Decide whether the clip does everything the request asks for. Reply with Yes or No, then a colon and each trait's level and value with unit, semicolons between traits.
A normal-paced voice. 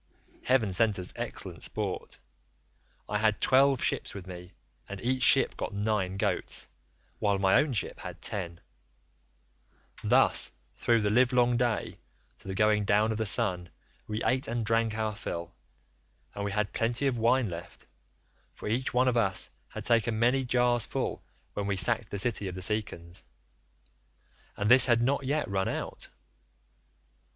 Yes: average, 160 wpm